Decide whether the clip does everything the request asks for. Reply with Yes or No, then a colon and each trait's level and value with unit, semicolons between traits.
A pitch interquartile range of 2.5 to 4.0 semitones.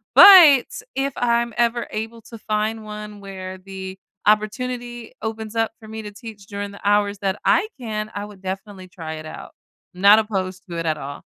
Yes: average, 2.8 semitones